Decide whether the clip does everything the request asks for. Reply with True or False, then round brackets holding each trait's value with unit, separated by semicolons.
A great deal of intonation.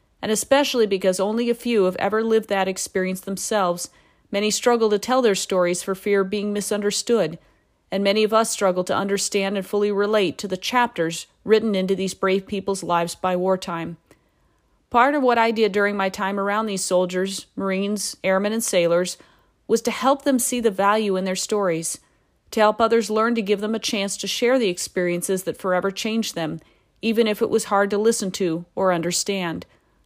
False (2.8 semitones)